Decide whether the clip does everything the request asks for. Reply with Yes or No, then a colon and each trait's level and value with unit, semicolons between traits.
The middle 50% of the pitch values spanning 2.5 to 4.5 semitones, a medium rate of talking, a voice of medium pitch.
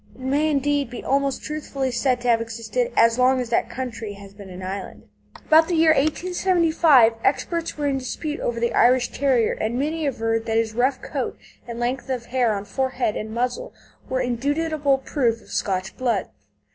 No: average, 4.1 semitones; average, 185 wpm; very high, 255 Hz